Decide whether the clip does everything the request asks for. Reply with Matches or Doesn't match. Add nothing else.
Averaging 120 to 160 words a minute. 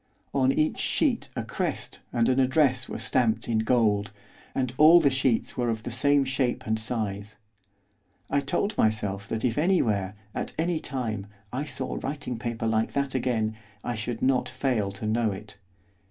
Doesn't match